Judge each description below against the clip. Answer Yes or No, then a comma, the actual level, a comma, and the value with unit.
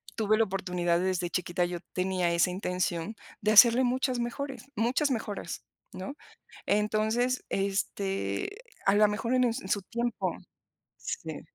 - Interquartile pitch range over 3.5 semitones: Yes, average, 4.4 semitones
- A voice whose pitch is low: No, high, 210 Hz